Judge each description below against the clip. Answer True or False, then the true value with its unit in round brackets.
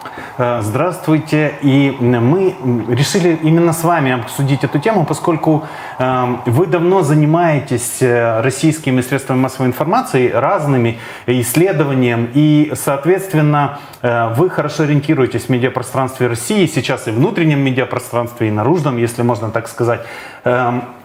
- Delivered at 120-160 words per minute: False (110 wpm)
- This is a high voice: False (135 Hz)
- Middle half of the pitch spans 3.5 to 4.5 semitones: True (4.1 semitones)